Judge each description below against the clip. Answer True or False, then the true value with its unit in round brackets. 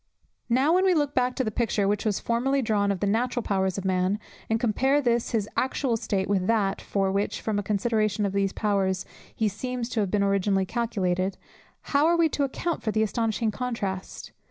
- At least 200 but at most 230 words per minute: True (205 wpm)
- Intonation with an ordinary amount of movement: True (3.9 semitones)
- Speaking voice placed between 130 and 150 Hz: False (215 Hz)